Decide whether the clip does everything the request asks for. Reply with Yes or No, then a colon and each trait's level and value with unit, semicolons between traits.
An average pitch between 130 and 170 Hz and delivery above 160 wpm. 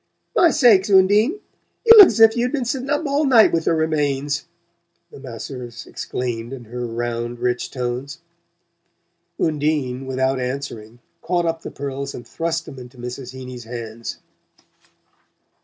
No: low, 135 Hz; average, 140 wpm